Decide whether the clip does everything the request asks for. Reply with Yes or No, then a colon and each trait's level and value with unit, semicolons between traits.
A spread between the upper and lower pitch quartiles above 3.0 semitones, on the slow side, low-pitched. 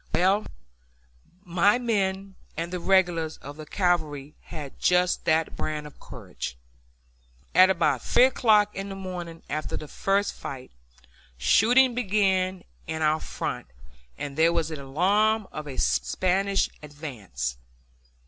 No: average, 4.3 semitones; slow, 130 wpm; medium, 175 Hz